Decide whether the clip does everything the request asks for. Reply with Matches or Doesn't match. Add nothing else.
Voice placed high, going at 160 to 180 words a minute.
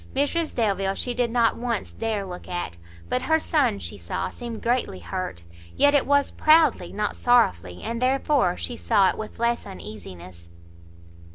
Matches